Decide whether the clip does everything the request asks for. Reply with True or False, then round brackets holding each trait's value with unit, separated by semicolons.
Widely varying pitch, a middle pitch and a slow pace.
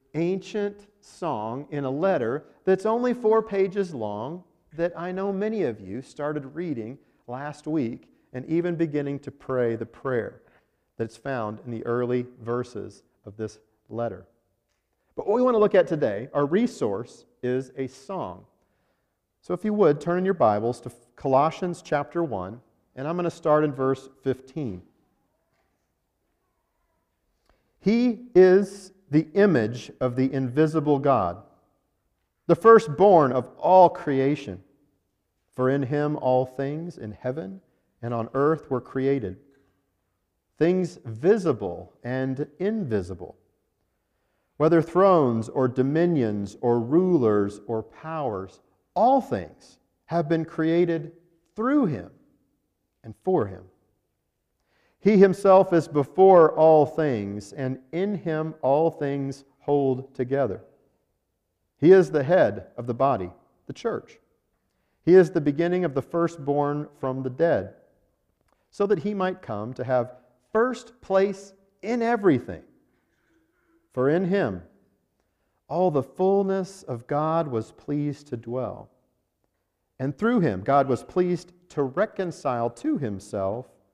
True (6.3 semitones; 145 Hz; 130 wpm)